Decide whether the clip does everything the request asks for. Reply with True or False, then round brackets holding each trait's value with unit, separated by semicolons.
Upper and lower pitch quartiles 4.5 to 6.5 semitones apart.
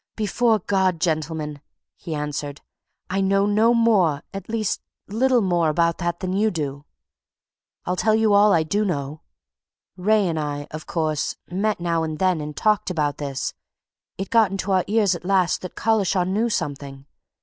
True (4.9 semitones)